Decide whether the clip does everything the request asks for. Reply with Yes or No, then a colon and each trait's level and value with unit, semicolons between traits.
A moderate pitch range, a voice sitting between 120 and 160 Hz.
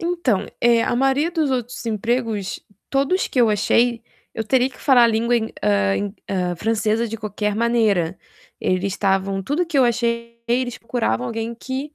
No: average, 3.6 semitones; high, 230 Hz